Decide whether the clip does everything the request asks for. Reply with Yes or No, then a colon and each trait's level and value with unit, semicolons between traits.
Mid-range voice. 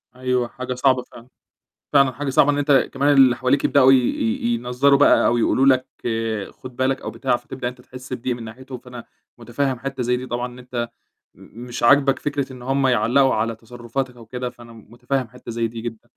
No: low, 125 Hz